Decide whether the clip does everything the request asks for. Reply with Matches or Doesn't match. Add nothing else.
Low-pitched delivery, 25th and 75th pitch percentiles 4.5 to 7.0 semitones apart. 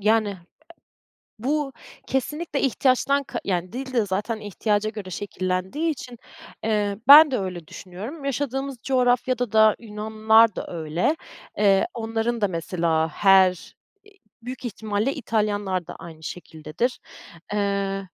Doesn't match